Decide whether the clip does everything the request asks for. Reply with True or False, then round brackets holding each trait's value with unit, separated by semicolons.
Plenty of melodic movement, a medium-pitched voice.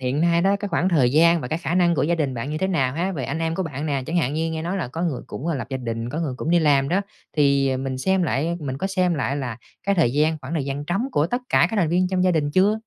False (4.2 semitones; 160 Hz)